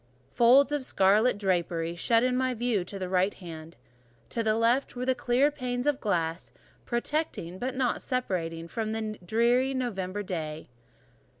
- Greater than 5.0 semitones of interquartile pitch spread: Yes, wide, 5.6 semitones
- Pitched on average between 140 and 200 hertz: No, high, 225 Hz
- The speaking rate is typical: Yes, average, 165 wpm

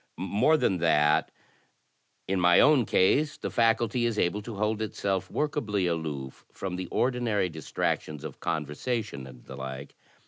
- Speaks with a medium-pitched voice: No, very low, 95 Hz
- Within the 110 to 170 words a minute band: Yes, average, 145 wpm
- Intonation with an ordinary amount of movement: No, wide, 6.5 semitones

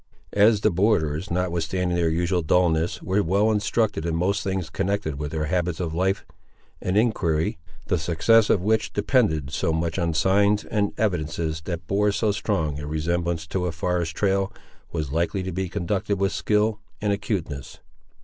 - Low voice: Yes, very low, 90 Hz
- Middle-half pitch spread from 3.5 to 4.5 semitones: Yes, average, 3.9 semitones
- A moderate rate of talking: Yes, average, 170 wpm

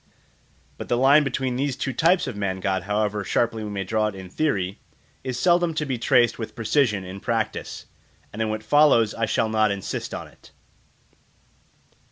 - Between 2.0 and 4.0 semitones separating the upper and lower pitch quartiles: No, average, 4.4 semitones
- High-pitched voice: No, low, 110 Hz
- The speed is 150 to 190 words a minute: Yes, average, 185 wpm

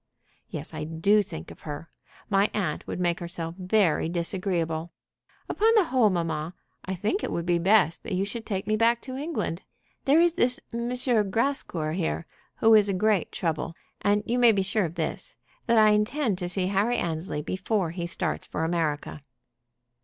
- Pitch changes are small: No, average, 4.6 semitones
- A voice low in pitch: No, high, 190 Hz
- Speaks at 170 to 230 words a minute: Yes, average, 185 wpm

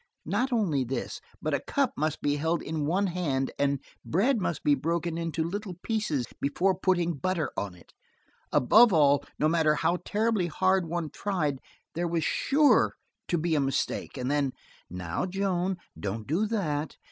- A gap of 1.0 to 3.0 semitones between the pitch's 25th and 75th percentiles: No, average, 4.7 semitones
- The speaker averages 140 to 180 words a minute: Yes, average, 170 wpm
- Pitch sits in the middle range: Yes, medium, 165 Hz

